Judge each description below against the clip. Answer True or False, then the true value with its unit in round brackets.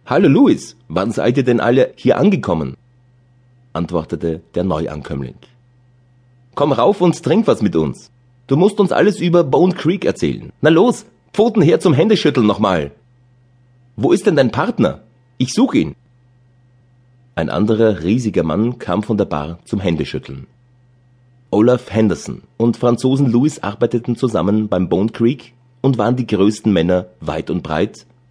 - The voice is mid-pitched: False (125 Hz)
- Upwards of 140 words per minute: True (150 wpm)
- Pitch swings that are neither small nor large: True (3.5 semitones)